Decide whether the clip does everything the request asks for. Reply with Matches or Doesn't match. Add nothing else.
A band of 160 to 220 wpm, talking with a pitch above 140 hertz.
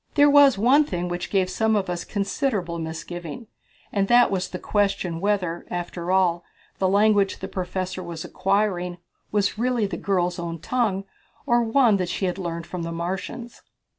Matches